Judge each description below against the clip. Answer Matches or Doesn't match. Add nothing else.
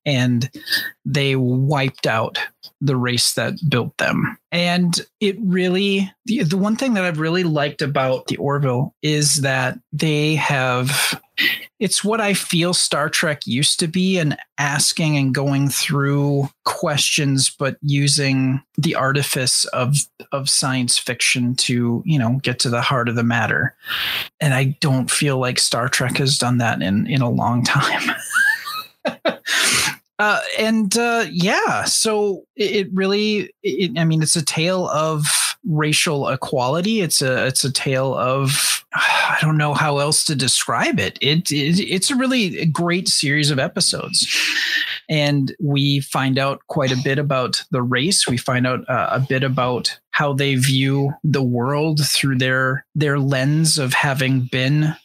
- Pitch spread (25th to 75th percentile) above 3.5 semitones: Matches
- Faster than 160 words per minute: Doesn't match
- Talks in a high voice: Doesn't match